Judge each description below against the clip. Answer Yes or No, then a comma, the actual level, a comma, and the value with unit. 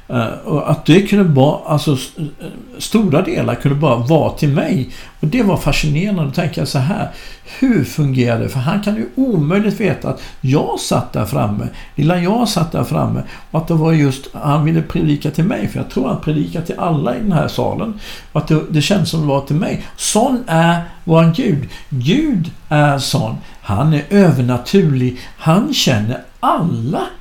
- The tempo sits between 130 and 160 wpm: No, average, 190 wpm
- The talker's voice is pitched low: No, medium, 160 Hz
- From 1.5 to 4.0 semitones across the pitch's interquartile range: No, average, 5.2 semitones